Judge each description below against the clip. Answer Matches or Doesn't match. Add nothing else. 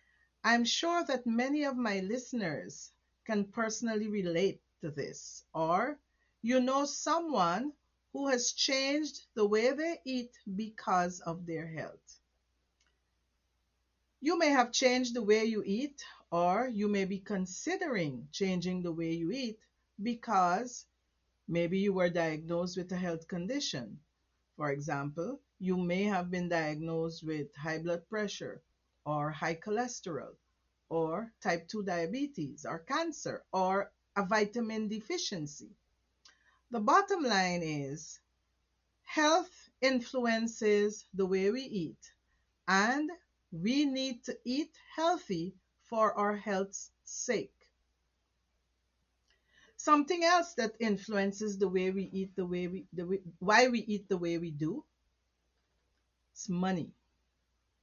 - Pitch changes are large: Matches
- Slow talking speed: Matches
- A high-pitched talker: Matches